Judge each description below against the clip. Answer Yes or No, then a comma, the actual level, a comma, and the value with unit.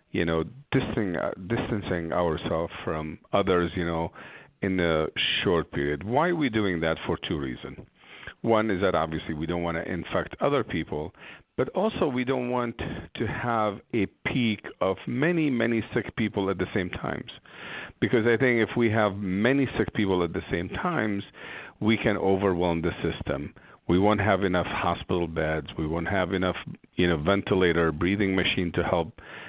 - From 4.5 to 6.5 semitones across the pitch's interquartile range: Yes, average, 4.9 semitones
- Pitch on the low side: Yes, very low, 95 Hz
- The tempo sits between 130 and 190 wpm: Yes, average, 175 wpm